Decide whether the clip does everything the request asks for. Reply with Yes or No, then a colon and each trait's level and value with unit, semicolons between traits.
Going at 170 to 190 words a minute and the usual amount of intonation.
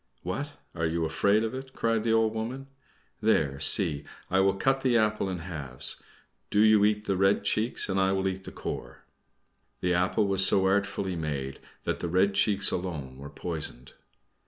Yes: average, 180 wpm; average, 4.2 semitones